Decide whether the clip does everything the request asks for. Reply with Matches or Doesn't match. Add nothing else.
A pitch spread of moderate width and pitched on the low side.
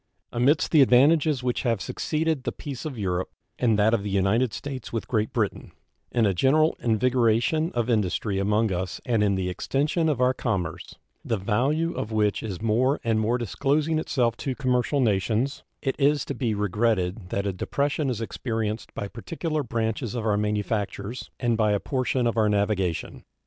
Matches